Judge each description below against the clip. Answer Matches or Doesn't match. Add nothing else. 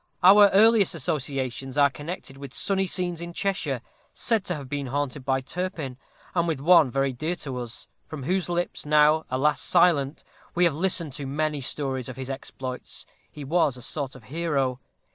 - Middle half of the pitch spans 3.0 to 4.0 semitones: Doesn't match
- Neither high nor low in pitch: Matches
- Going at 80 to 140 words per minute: Doesn't match